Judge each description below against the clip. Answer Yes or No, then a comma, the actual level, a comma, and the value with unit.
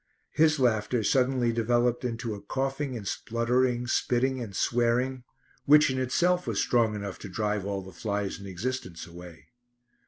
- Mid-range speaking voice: No, low, 120 Hz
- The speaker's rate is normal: Yes, average, 155 wpm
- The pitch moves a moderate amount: Yes, average, 3.9 semitones